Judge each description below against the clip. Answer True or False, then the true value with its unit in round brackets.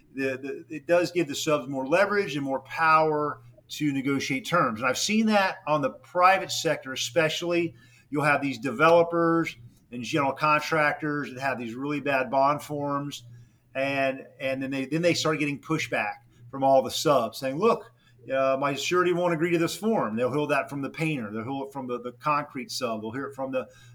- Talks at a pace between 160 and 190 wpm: False (200 wpm)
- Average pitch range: True (3.1 semitones)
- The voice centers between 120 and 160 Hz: True (140 Hz)